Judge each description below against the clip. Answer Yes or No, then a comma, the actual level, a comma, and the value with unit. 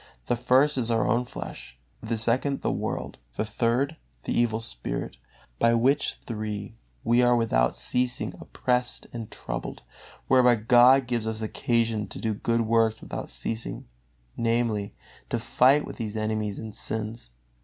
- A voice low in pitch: Yes, low, 115 Hz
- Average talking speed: Yes, average, 150 wpm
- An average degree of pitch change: No, narrow, 2.0 semitones